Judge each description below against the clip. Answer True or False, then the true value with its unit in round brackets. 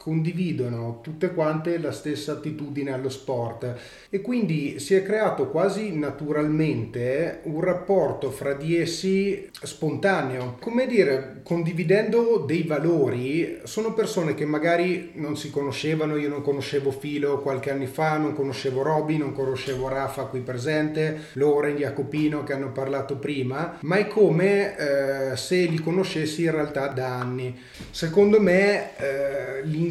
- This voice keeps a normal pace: True (135 wpm)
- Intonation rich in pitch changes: False (3.9 semitones)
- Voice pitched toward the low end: False (150 Hz)